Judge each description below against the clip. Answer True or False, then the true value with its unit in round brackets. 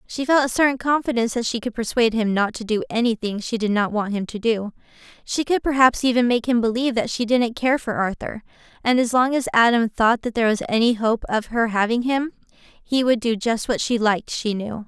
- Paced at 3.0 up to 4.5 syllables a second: False (5.6 syllables/s)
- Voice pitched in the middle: False (235 Hz)